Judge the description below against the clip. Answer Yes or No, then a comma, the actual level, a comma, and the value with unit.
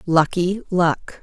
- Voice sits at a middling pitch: Yes, medium, 175 Hz